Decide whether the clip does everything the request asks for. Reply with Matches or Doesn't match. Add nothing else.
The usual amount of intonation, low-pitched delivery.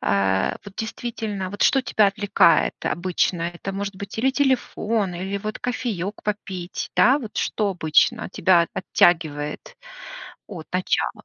Doesn't match